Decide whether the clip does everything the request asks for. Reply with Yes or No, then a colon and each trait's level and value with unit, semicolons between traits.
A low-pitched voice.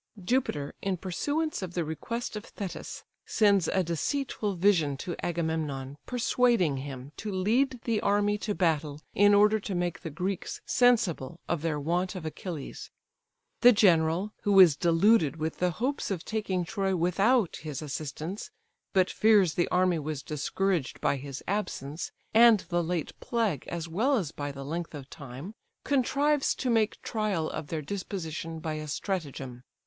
No: medium, 180 Hz